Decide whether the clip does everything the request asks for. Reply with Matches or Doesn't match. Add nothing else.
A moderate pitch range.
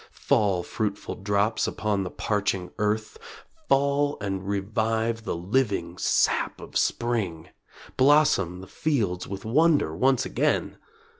Matches